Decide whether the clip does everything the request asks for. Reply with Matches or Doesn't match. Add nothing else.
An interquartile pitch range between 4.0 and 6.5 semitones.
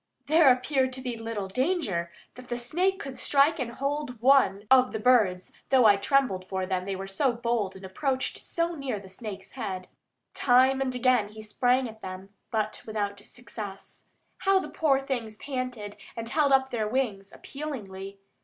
Matches